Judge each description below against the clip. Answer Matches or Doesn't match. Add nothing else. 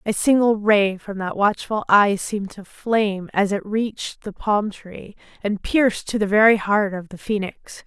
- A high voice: Matches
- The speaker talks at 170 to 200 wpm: Matches